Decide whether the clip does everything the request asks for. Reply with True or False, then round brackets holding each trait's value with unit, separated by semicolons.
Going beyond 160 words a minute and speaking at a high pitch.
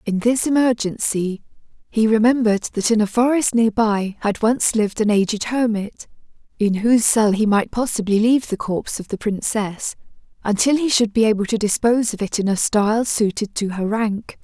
True (185 wpm; 220 Hz)